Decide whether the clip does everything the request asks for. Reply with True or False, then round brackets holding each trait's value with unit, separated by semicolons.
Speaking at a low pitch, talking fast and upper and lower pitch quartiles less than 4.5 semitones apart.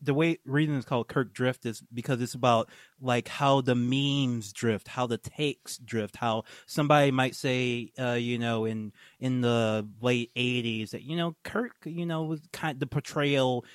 False (125 Hz; 190 wpm; 3.4 semitones)